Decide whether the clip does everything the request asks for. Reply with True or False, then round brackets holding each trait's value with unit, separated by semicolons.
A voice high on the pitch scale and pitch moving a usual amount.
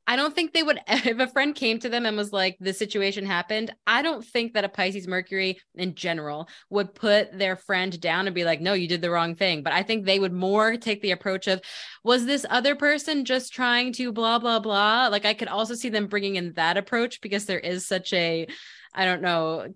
True (200 Hz; 4.1 semitones)